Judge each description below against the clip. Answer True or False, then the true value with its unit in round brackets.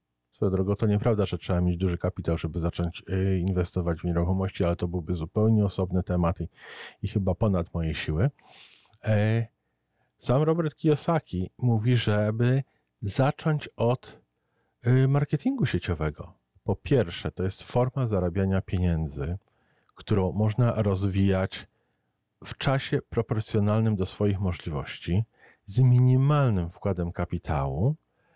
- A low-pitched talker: True (95 Hz)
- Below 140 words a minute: True (110 wpm)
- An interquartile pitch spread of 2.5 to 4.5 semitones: False (4.9 semitones)